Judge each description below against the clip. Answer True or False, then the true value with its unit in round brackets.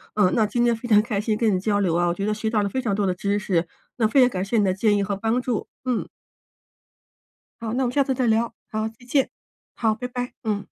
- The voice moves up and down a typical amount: True (3.0 semitones)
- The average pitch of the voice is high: True (220 Hz)